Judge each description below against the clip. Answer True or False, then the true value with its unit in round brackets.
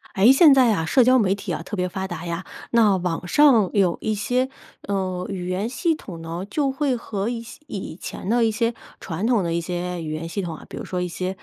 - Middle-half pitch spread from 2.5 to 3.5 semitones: False (4.7 semitones)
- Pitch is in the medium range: False (195 Hz)